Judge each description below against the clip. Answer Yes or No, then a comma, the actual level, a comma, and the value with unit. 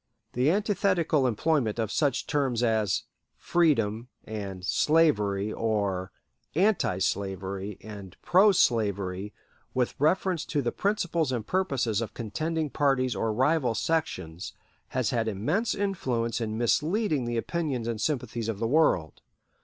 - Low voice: Yes, low, 120 Hz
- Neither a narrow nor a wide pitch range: No, wide, 6.8 semitones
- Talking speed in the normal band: No, slow, 130 wpm